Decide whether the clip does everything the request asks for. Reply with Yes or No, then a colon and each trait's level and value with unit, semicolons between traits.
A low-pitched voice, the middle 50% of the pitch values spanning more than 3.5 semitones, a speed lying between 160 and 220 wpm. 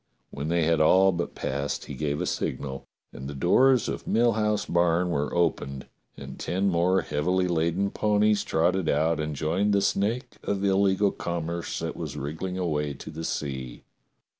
Yes: very low, 85 Hz; average, 4.4 semitones; average, 175 wpm